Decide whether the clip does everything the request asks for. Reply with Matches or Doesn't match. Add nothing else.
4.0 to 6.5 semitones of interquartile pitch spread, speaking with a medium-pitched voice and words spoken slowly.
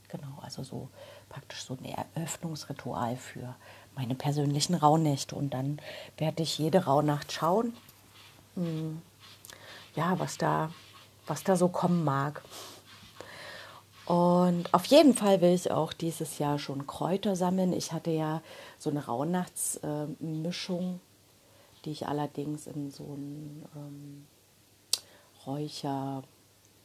Matches